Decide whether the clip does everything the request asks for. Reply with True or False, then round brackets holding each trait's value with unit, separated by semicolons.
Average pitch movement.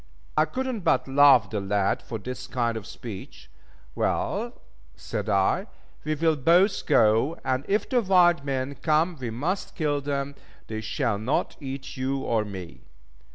False (6.0 semitones)